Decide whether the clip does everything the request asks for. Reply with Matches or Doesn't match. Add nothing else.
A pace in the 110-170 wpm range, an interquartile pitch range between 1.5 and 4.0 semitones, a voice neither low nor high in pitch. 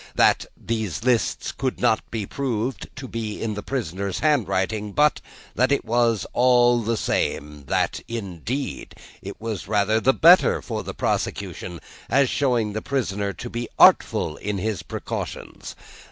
Doesn't match